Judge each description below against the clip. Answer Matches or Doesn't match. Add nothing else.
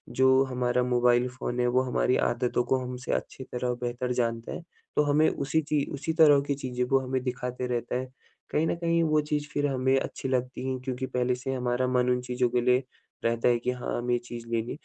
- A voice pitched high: Doesn't match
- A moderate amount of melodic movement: Doesn't match